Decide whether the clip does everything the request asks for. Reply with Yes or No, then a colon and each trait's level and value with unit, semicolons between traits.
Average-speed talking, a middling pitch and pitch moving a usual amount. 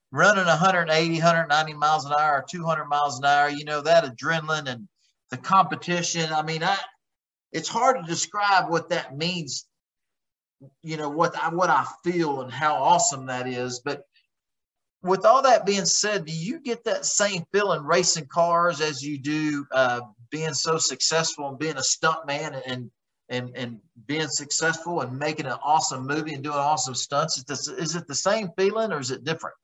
Yes: average, 185 wpm; medium, 155 Hz; average, 3.4 semitones